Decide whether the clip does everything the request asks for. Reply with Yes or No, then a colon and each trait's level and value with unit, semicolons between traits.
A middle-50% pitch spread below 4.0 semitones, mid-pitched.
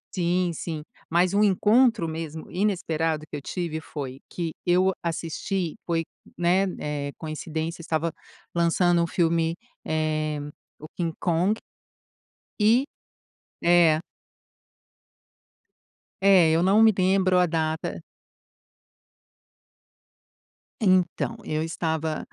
Yes: narrow, 2.5 semitones; medium, 170 Hz